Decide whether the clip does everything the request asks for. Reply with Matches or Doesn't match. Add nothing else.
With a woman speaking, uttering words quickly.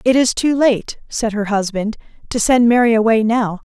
Doesn't match